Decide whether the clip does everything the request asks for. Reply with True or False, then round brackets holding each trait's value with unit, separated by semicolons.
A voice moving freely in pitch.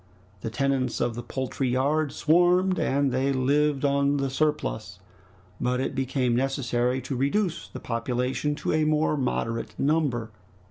False (2.9 semitones)